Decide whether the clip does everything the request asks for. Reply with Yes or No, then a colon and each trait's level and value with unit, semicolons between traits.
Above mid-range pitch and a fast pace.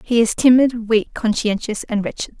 No: high, 225 Hz; average, 175 wpm